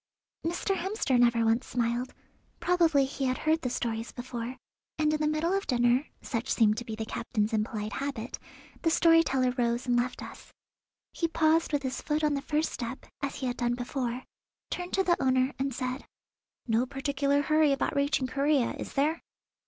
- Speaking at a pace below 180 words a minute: No, average, 185 wpm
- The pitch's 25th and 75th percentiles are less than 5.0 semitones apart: Yes, average, 4.0 semitones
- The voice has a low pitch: No, very high, 265 Hz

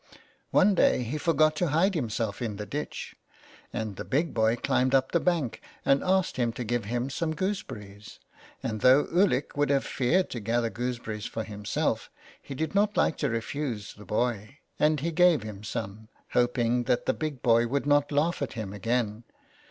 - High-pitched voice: No, low, 125 Hz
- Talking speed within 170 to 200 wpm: Yes, average, 185 wpm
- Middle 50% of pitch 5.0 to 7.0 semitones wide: Yes, average, 5.3 semitones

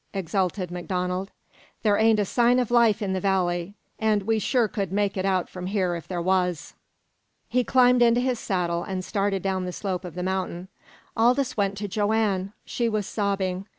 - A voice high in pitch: Yes, high, 195 Hz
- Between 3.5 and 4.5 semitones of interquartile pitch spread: No, average, 3.1 semitones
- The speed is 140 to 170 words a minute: No, average, 185 wpm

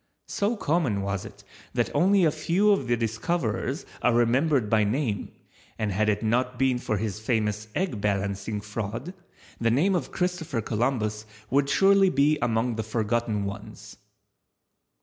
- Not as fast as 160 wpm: Yes, average, 150 wpm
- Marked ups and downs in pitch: Yes, wide, 5.8 semitones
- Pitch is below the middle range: Yes, low, 120 Hz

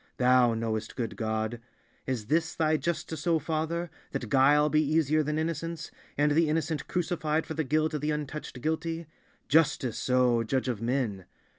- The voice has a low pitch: No, medium, 150 Hz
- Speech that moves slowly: No, average, 155 wpm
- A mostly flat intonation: No, average, 4.2 semitones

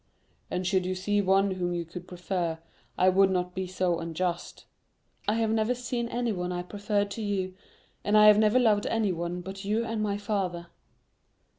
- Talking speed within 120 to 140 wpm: No, average, 180 wpm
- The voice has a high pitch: Yes, high, 195 Hz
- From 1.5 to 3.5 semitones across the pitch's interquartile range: Yes, average, 2.9 semitones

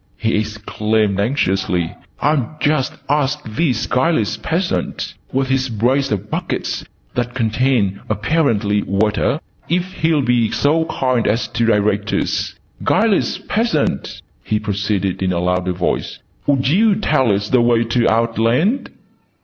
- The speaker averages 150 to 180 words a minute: No, slow, 135 wpm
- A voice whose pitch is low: Yes, low, 115 Hz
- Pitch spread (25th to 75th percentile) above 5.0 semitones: Yes, wide, 5.5 semitones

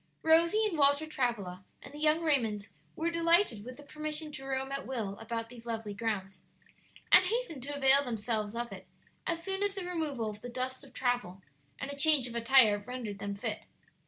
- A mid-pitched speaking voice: No, very high, 260 Hz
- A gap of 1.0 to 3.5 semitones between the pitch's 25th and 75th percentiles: No, wide, 5.5 semitones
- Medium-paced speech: Yes, average, 195 wpm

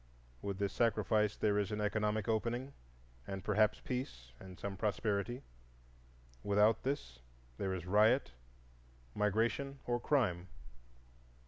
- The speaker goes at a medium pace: No, slow, 115 wpm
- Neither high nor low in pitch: No, low, 105 Hz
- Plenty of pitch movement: No, average, 2.9 semitones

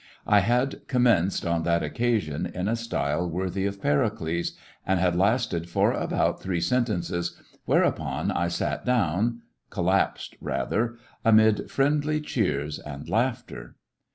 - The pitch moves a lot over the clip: Yes, wide, 5.8 semitones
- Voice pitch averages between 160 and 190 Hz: No, very low, 95 Hz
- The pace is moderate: No, slow, 125 wpm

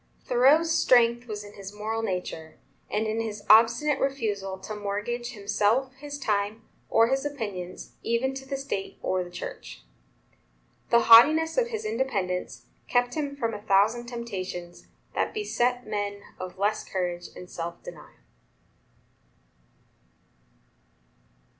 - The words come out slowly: Yes, slow, 130 wpm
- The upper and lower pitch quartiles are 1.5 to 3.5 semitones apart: No, average, 4.7 semitones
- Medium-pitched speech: No, high, 225 Hz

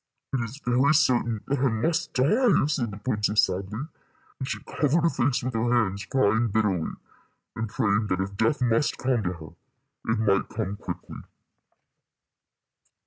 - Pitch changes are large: No, average, 4.1 semitones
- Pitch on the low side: Yes, low, 115 Hz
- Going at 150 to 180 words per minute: Yes, average, 160 wpm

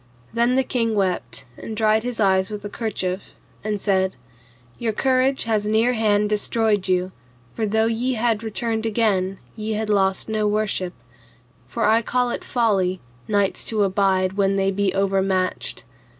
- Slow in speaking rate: No, average, 160 wpm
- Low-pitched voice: No, high, 210 Hz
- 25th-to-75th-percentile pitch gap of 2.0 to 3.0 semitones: Yes, narrow, 2.5 semitones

